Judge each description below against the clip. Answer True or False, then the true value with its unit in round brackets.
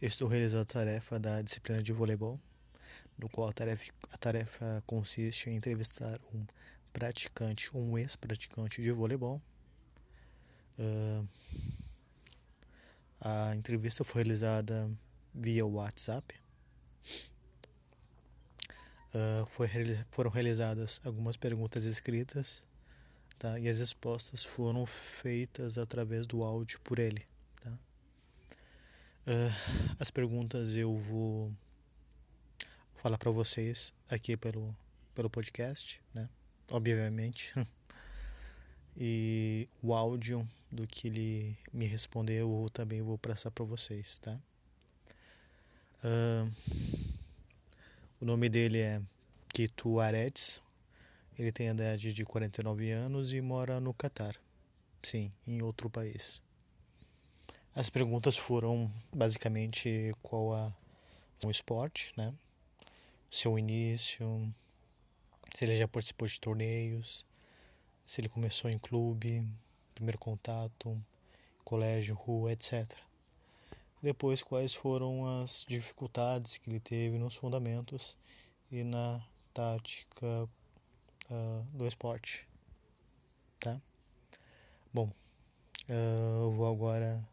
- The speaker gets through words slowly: True (100 wpm)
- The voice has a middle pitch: False (115 Hz)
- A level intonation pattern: True (1.5 semitones)